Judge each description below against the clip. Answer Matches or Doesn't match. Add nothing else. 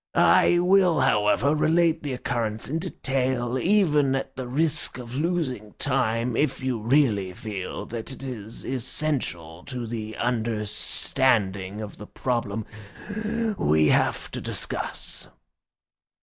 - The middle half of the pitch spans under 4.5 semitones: Doesn't match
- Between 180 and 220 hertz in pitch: Doesn't match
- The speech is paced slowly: Matches